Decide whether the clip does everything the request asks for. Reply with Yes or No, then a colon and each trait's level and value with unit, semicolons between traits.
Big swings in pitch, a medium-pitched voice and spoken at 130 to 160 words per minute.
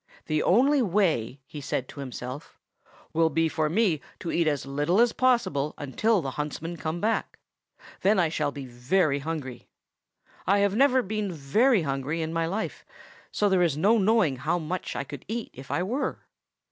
No: wide, 6.2 semitones; medium, 165 Hz; average, 180 wpm